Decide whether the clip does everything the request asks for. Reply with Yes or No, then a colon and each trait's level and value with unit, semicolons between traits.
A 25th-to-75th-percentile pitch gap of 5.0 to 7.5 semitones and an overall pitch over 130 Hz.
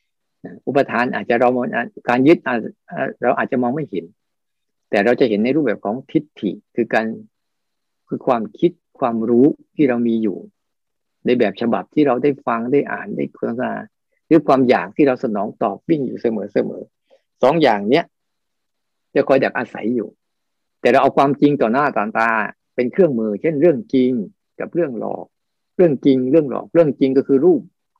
Yes: wide, 5.5 semitones; medium, 140 Hz